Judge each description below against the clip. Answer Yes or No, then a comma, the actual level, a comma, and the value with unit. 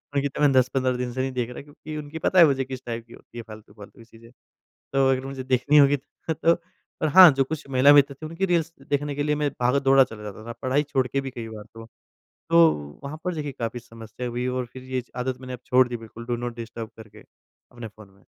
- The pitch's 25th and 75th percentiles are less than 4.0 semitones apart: Yes, average, 3.4 semitones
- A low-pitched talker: Yes, low, 130 Hz